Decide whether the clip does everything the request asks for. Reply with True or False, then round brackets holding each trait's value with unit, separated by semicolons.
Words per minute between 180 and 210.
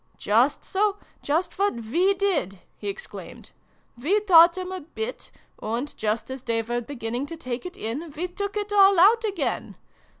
True (190 wpm)